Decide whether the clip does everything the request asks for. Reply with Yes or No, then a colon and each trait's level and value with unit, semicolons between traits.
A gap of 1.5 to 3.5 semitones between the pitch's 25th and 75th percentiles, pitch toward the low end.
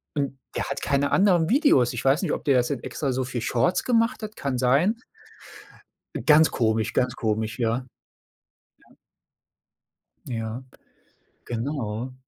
No: average, 4.8 semitones; low, 130 Hz